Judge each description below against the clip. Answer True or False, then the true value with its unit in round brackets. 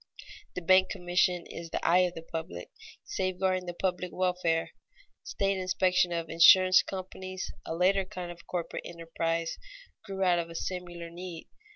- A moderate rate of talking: True (155 wpm)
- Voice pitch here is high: False (180 Hz)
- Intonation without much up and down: True (1.8 semitones)